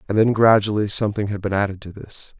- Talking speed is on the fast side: Yes, fast, 225 wpm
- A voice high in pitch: No, low, 105 Hz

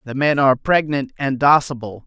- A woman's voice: No, male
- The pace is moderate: Yes, average, 175 wpm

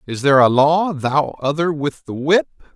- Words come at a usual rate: Yes, average, 195 wpm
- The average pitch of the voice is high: No, medium, 145 Hz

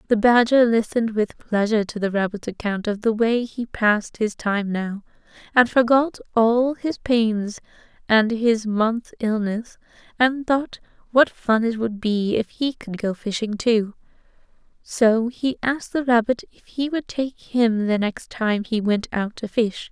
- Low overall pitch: No, high, 225 Hz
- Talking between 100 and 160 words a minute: No, average, 170 wpm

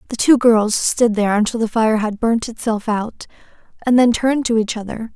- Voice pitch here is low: No, high, 225 Hz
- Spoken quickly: Yes, fast, 210 wpm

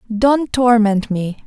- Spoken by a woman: Yes, female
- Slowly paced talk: Yes, slow, 125 wpm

